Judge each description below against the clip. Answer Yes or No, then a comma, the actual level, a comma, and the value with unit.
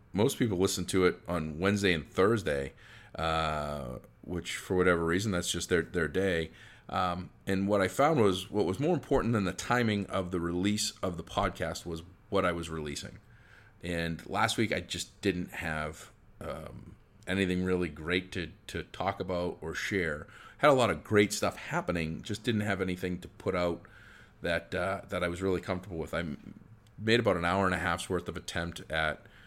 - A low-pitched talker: Yes, very low, 90 Hz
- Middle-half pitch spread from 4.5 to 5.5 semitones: No, average, 2.7 semitones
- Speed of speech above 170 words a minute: Yes, average, 190 wpm